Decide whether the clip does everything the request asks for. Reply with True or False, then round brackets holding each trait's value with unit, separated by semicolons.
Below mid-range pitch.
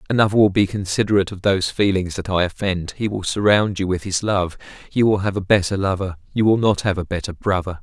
True (95 Hz)